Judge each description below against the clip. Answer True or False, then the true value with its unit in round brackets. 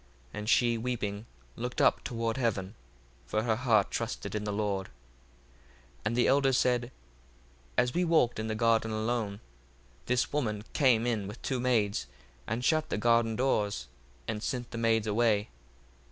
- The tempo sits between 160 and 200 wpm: True (165 wpm)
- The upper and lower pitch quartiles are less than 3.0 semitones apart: True (2.5 semitones)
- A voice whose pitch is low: True (115 Hz)